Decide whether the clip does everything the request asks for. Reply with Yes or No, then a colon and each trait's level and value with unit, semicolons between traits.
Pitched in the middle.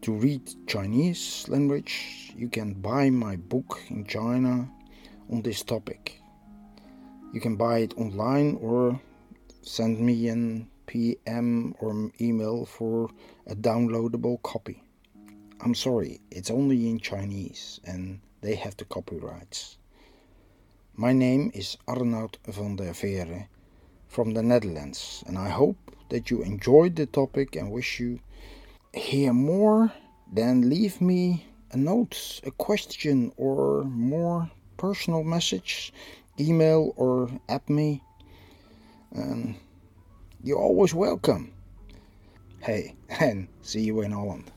No: low, 115 Hz